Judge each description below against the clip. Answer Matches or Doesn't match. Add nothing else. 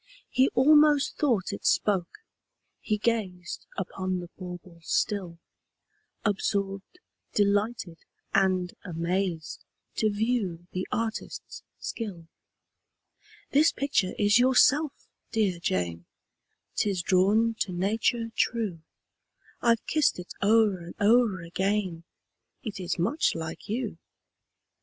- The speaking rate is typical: Doesn't match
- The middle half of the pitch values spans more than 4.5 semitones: Doesn't match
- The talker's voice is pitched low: Doesn't match